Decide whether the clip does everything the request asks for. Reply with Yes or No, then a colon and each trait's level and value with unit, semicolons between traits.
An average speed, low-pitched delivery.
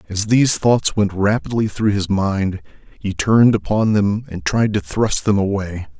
Yes: average, 180 wpm; low, 100 Hz